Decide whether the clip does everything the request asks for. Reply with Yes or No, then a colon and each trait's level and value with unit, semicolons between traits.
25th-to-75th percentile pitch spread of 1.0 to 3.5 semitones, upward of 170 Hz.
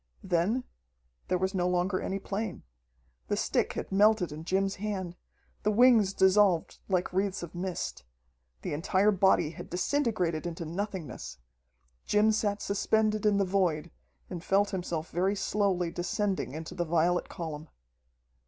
Yes: average, 2.9 semitones; high, 190 Hz